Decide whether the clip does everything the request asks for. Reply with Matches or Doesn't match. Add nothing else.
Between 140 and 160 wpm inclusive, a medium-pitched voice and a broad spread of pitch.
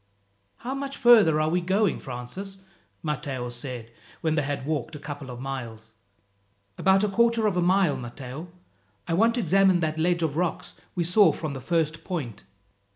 Doesn't match